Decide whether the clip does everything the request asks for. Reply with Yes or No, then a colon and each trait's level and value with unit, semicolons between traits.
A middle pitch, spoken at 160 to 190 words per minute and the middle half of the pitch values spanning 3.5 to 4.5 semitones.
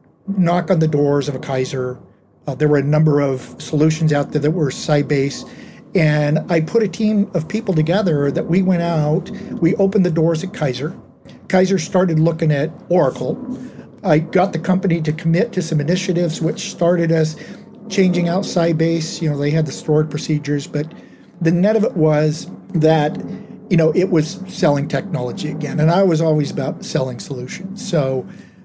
Yes: medium, 165 Hz; average, 180 wpm; average, 3.8 semitones